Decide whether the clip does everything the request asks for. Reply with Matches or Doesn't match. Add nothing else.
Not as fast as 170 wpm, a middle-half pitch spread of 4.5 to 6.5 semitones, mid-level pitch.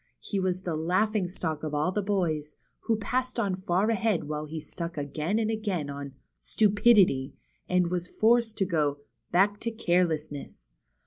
Doesn't match